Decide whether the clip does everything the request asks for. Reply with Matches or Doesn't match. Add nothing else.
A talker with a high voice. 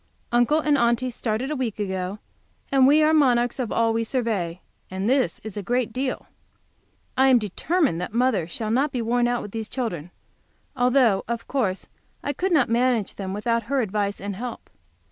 Matches